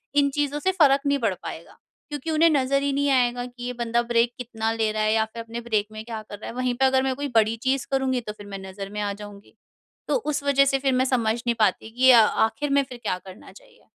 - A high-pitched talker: Yes, high, 245 Hz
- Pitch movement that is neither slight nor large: Yes, average, 4.0 semitones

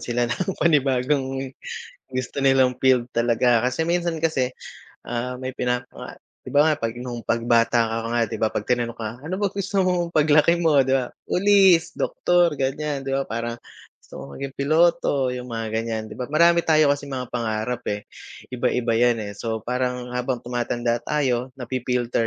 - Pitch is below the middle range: Yes, low, 125 Hz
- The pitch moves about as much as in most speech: Yes, average, 3.8 semitones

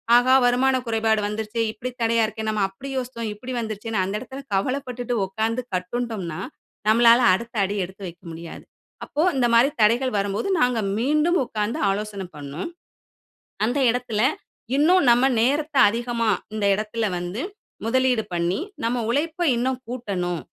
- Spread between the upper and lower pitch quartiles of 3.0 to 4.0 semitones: Yes, average, 3.4 semitones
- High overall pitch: Yes, high, 230 Hz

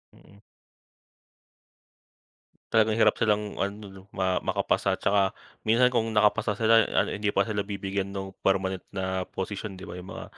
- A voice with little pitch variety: Yes, narrow, 1.9 semitones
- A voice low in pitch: Yes, low, 100 Hz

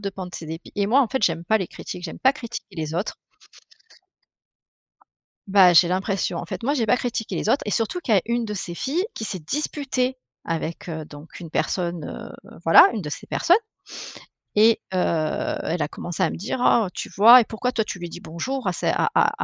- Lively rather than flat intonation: Yes, wide, 5.8 semitones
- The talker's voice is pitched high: Yes, high, 200 Hz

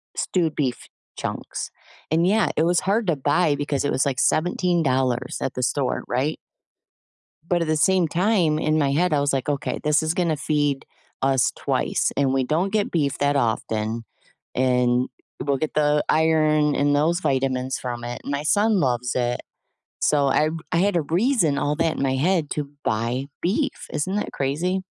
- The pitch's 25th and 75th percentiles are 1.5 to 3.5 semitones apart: No, average, 4.1 semitones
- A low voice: No, medium, 150 Hz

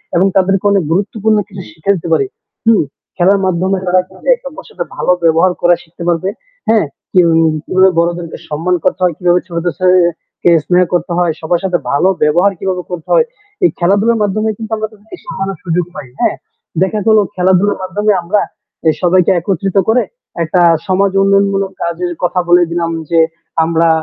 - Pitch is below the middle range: No, medium, 185 Hz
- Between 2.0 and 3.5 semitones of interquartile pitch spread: Yes, narrow, 2.4 semitones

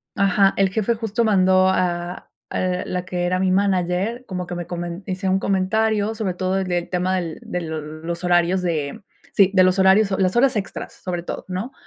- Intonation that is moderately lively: No, narrow, 1.8 semitones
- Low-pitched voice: No, medium, 185 Hz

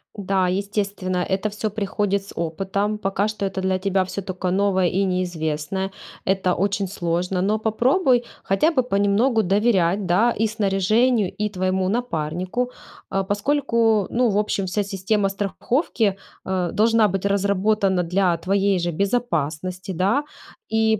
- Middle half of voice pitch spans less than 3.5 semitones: Yes, narrow, 2.5 semitones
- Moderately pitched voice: No, high, 195 Hz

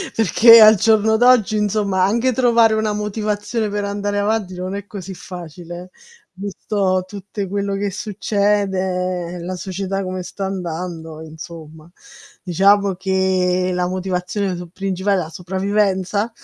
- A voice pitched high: Yes, high, 195 Hz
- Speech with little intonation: Yes, narrow, 2.2 semitones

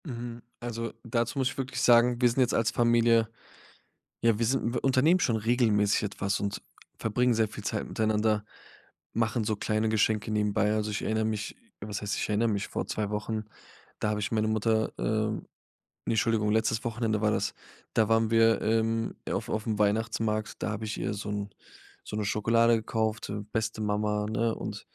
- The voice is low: Yes, low, 110 Hz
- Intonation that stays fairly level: Yes, narrow, 1.5 semitones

